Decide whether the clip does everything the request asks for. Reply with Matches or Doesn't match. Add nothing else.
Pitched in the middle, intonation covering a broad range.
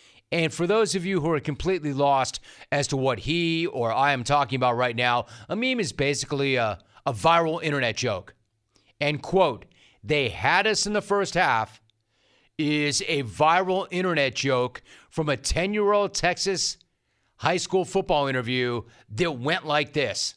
Matches